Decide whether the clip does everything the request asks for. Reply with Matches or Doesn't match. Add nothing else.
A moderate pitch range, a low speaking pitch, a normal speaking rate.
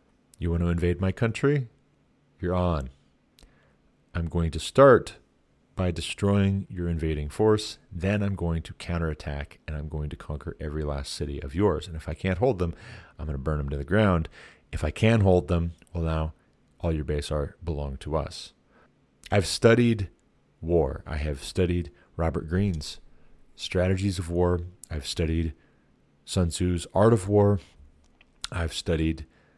Matches